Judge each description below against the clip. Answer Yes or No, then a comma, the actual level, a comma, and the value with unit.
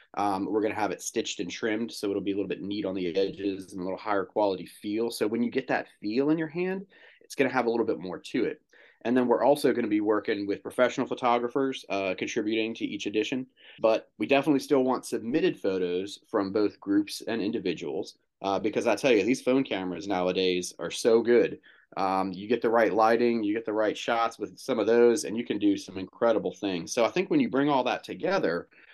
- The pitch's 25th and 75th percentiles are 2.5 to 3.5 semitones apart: No, average, 4.6 semitones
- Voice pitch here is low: Yes, low, 115 Hz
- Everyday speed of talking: No, fast, 240 wpm